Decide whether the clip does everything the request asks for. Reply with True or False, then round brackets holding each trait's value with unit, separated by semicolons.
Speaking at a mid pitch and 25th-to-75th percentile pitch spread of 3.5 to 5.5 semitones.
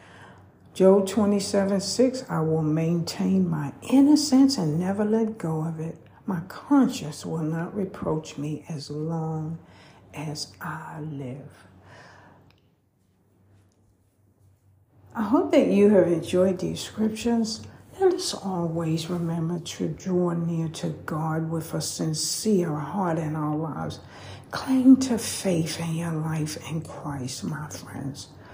True (160 Hz; 5.1 semitones)